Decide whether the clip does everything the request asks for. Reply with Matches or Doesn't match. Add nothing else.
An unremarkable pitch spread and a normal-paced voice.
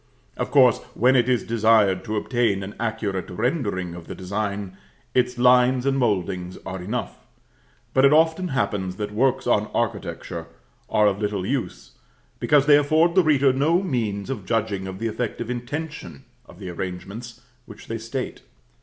Matches